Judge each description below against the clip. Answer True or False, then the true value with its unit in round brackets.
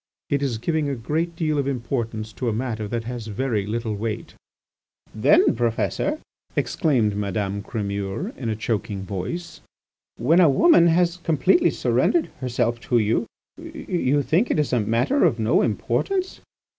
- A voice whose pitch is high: False (120 Hz)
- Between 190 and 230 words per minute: False (155 wpm)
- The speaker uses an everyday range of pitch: False (6.6 semitones)